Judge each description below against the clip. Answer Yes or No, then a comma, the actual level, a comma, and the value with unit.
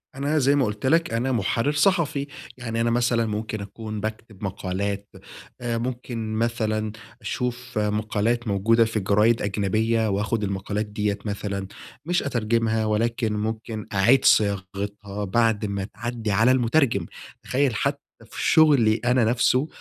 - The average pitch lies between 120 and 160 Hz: No, low, 110 Hz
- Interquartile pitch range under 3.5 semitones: Yes, average, 2.7 semitones